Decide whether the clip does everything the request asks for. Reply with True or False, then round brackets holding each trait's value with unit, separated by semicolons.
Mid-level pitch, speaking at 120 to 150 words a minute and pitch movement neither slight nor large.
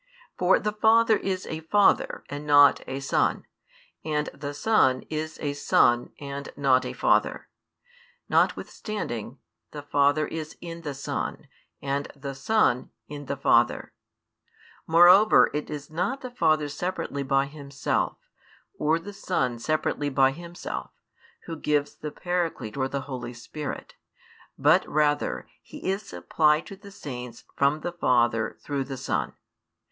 True (150 Hz; 140 wpm; 3.7 semitones)